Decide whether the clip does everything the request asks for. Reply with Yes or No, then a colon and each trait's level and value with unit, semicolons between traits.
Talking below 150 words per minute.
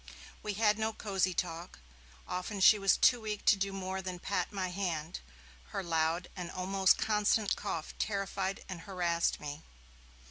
No: average, 155 wpm